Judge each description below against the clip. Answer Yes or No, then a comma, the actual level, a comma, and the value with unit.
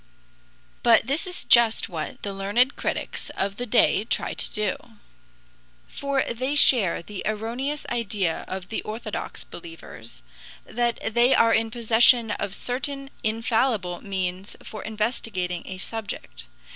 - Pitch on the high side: Yes, high, 225 Hz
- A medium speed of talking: No, slow, 130 wpm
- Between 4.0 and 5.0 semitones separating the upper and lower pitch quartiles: No, average, 3.6 semitones